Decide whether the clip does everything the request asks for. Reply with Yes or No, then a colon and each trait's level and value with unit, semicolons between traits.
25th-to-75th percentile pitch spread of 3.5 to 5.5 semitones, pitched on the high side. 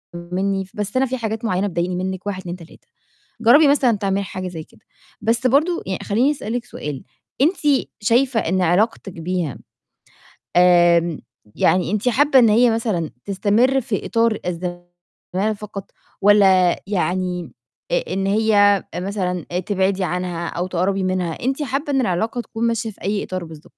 Yes: average, 4.1 semitones; high, 195 Hz